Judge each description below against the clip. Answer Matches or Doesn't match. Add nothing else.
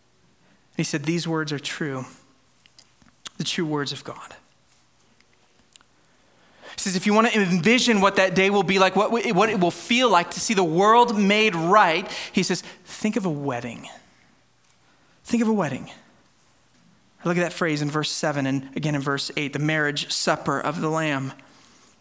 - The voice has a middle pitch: Matches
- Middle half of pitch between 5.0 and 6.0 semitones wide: Matches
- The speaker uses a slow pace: Doesn't match